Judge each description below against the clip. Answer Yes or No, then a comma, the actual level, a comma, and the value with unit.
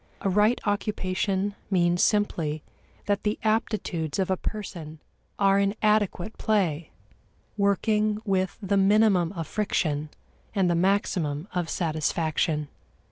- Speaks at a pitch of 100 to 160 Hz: No, high, 195 Hz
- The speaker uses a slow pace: Yes, slow, 120 wpm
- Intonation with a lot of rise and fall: No, average, 3.7 semitones